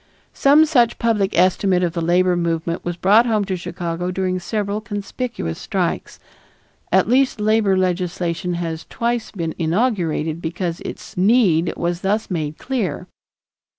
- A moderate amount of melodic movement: Yes, average, 4.0 semitones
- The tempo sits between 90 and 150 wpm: Yes, average, 140 wpm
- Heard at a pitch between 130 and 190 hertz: Yes, medium, 185 Hz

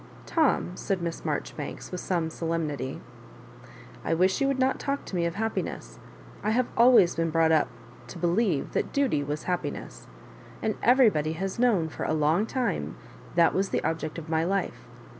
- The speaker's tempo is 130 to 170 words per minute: No, average, 180 wpm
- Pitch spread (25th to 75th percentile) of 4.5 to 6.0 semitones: Yes, wide, 5.4 semitones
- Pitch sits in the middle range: Yes, medium, 175 Hz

